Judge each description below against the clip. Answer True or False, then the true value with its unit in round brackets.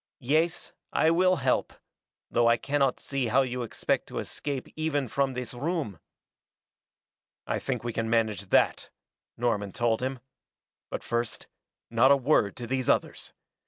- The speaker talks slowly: False (150 wpm)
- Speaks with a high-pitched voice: False (125 Hz)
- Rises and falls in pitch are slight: False (3.3 semitones)